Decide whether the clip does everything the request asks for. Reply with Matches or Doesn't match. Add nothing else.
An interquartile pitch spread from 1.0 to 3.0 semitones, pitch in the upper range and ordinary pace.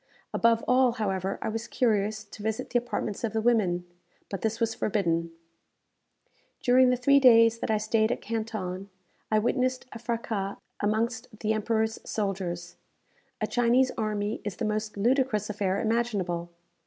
Matches